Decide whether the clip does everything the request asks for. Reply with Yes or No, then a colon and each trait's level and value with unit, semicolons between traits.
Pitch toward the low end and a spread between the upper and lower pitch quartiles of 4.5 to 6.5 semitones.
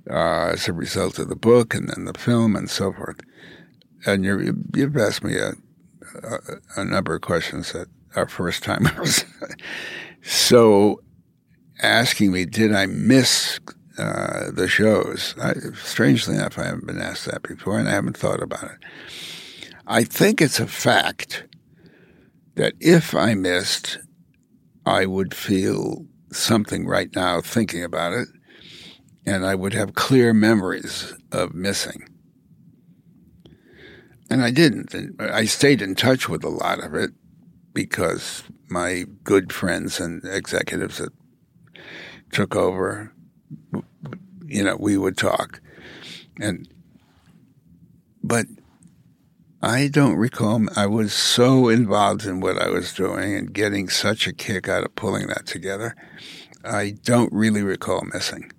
No: low, 105 Hz; average, 3.8 semitones